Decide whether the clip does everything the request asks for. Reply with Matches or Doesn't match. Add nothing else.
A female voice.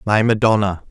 Doesn't match